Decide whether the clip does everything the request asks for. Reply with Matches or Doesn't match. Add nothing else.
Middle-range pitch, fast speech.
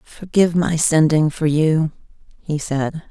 Doesn't match